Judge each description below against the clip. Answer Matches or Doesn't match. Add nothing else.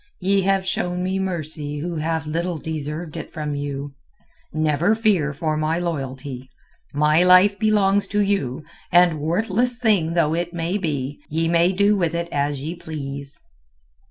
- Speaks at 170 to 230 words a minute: Doesn't match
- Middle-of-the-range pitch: Matches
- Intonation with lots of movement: Doesn't match